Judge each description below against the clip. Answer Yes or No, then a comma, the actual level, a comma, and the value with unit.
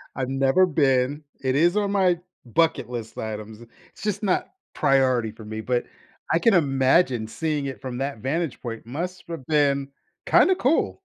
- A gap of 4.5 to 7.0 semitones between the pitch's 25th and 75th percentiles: Yes, wide, 5.4 semitones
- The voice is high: No, low, 135 Hz